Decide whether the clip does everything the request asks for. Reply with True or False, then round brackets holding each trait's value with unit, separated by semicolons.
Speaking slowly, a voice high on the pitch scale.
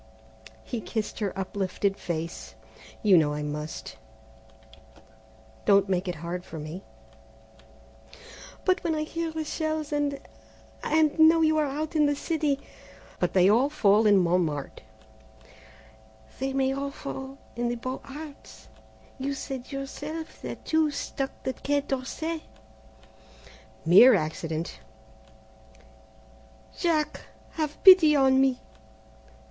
True (130 wpm; 265 Hz)